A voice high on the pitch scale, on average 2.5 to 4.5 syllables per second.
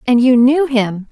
Yes: very high, 250 Hz; 4.1 syllables/s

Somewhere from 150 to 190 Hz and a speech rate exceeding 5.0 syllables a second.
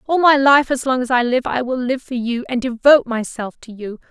No: very high, 250 Hz; 5.4 syllables/s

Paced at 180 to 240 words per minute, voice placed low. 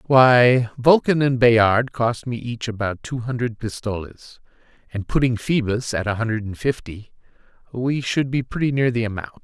No: average, 165 wpm; low, 120 Hz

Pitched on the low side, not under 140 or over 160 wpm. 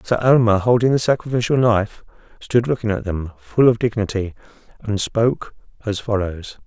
Yes: low, 110 Hz; average, 155 wpm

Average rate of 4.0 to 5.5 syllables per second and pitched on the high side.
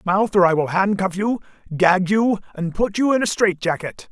Yes: 4.9 syllables/s; high, 195 Hz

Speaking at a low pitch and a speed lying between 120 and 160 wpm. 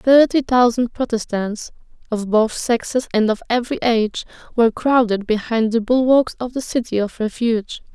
No: high, 235 Hz; average, 150 wpm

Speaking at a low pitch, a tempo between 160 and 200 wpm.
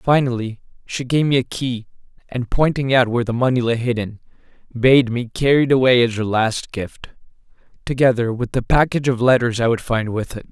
Yes: low, 125 Hz; average, 195 wpm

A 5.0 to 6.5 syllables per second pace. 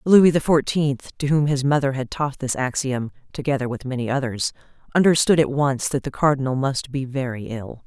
Yes: 5.2 syllables/s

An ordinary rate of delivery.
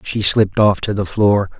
No: fast, 225 wpm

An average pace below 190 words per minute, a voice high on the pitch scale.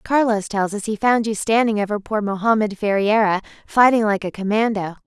Yes: average, 180 wpm; high, 210 Hz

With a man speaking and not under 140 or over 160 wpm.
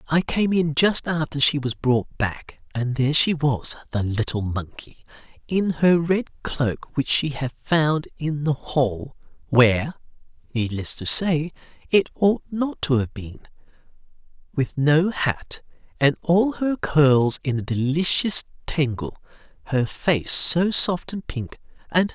Yes: male; average, 155 wpm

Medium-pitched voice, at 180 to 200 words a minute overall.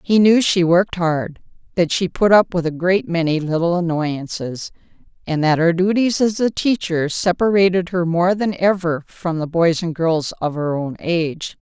Yes: medium, 175 Hz; average, 185 wpm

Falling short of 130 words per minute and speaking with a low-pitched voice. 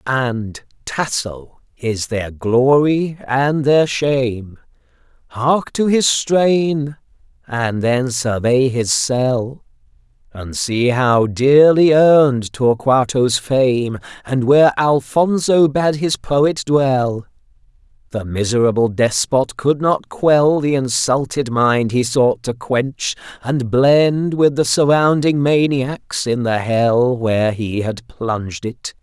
Yes: slow, 120 wpm; low, 130 Hz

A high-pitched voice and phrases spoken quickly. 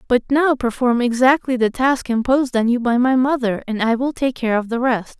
Yes: high, 245 Hz; fast, 230 wpm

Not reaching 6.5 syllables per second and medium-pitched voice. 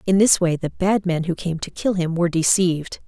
Yes: 5.5 syllables/s; medium, 175 Hz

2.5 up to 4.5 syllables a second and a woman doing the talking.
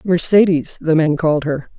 No: 5.0 syllables/s; female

